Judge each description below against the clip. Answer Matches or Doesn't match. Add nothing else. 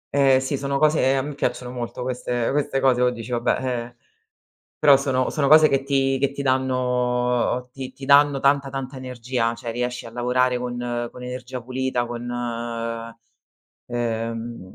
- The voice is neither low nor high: Doesn't match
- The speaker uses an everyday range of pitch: Doesn't match